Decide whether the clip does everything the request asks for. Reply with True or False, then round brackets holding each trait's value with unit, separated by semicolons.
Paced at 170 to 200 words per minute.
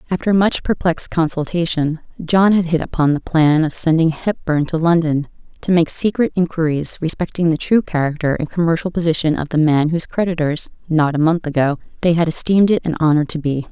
True (190 wpm)